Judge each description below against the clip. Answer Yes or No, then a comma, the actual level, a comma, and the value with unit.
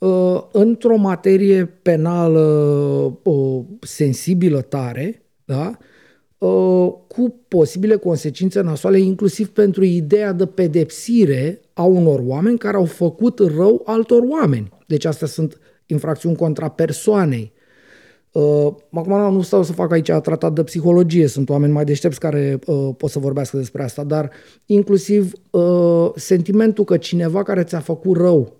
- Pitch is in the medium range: Yes, medium, 170 Hz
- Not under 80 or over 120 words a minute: No, average, 135 wpm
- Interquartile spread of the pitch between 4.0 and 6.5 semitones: Yes, average, 4.7 semitones